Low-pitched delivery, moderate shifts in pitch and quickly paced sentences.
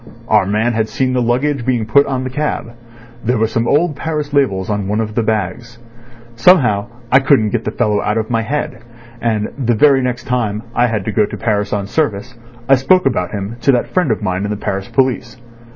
Yes: low, 115 Hz; average, 3.8 semitones; fast, 220 wpm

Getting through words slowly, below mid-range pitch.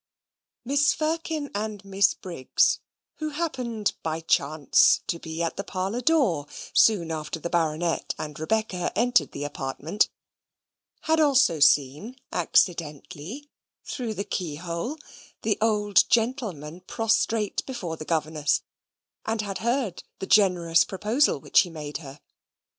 No: slow, 125 wpm; high, 190 Hz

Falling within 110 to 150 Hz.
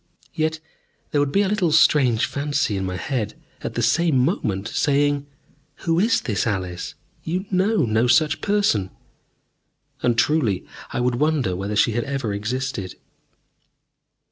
Yes: low, 135 Hz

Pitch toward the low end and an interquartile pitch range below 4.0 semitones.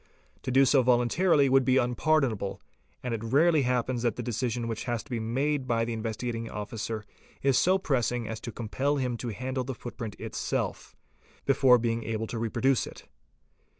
Yes: low, 120 Hz; narrow, 2.6 semitones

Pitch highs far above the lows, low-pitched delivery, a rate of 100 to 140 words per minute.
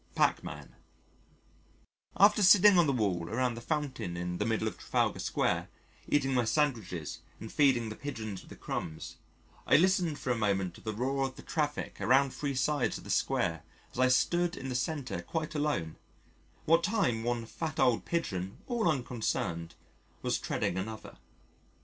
No: wide, 5.8 semitones; low, 125 Hz; average, 170 wpm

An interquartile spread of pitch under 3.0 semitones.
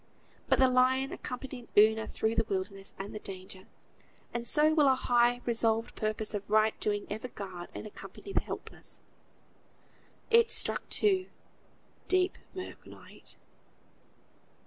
No: average, 4.0 semitones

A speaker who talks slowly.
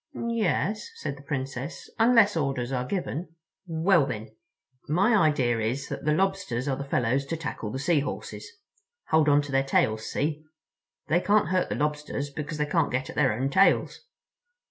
No: average, 170 wpm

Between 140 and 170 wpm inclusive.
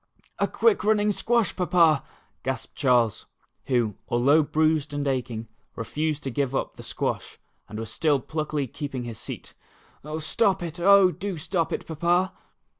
Yes: average, 155 wpm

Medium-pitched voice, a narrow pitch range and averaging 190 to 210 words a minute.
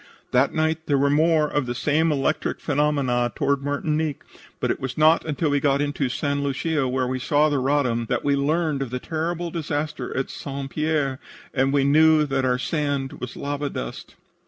Yes: medium, 145 Hz; narrow, 2.3 semitones; average, 195 wpm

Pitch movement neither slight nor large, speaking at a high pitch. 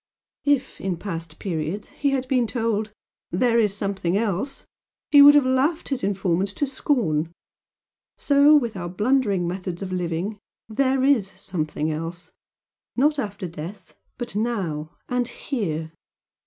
No: wide, 6.8 semitones; high, 205 Hz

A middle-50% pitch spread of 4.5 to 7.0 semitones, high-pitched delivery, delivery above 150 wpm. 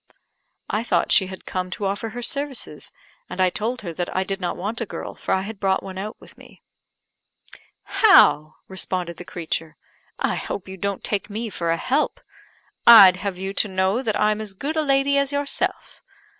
No: average, 4.0 semitones; high, 200 Hz; average, 200 wpm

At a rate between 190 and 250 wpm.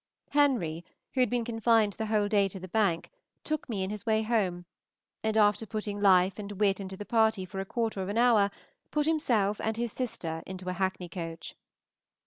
Yes: average, 200 wpm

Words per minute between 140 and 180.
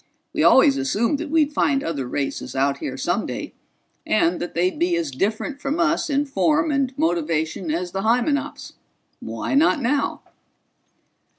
Yes: average, 155 wpm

